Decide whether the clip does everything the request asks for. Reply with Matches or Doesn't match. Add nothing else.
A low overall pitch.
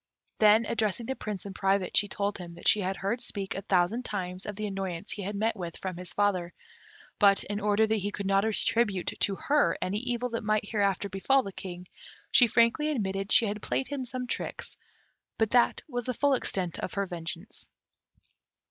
Doesn't match